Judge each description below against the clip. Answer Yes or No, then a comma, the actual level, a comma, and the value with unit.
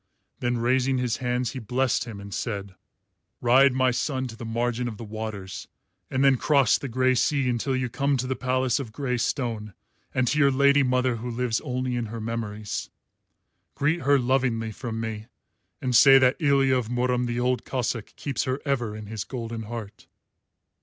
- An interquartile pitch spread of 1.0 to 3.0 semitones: Yes, narrow, 2.5 semitones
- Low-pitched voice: Yes, low, 125 Hz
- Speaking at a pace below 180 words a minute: No, average, 185 wpm